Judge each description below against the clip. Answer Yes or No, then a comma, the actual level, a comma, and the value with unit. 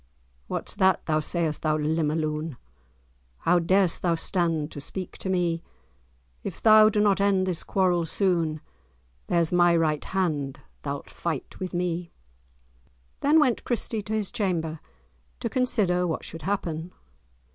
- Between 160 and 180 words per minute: No, average, 145 wpm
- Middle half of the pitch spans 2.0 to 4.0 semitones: Yes, average, 3.2 semitones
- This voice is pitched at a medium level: Yes, medium, 175 Hz